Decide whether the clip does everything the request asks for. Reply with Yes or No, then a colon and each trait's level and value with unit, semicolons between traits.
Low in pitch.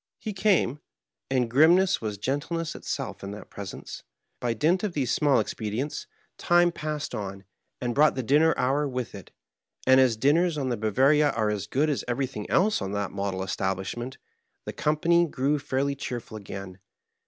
Yes: low, 130 Hz